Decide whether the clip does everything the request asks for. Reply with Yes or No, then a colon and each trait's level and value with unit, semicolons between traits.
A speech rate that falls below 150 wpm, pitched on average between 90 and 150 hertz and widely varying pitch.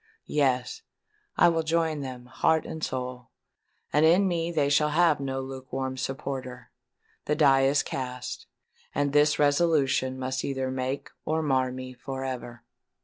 No: average, 140 wpm; low, 135 Hz; average, 2.9 semitones